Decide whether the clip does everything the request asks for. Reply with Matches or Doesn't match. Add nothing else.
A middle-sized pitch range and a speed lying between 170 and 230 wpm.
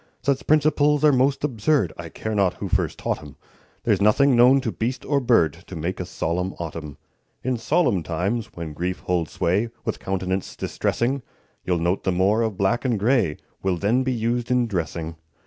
Doesn't match